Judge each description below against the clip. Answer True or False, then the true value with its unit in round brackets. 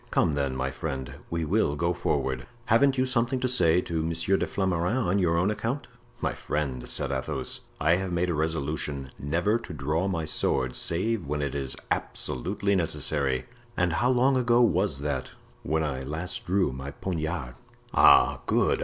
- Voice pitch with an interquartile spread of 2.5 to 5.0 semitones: False (5.6 semitones)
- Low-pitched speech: True (85 Hz)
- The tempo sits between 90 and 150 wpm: False (175 wpm)